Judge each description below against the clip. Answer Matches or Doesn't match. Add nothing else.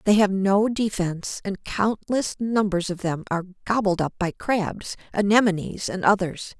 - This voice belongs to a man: Doesn't match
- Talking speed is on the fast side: Doesn't match